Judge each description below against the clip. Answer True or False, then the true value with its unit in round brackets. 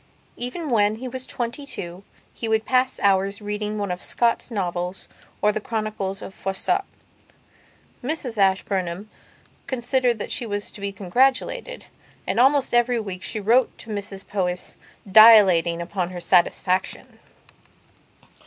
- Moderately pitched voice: False (210 Hz)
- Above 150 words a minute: False (135 wpm)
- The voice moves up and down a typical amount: True (4.0 semitones)